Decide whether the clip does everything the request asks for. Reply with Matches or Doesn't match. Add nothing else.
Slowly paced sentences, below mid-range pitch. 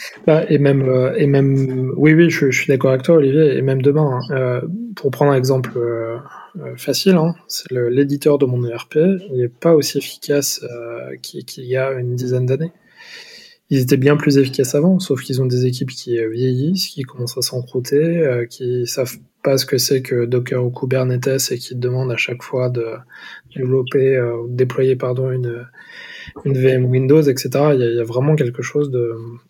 Doesn't match